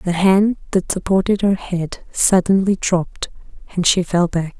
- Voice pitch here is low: No, medium, 185 Hz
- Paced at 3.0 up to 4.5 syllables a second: Yes, 4.4 syllables/s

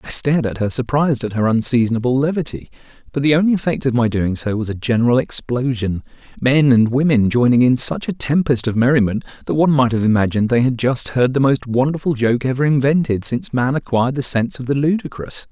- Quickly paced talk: Yes, fast, 210 wpm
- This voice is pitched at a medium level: No, low, 130 Hz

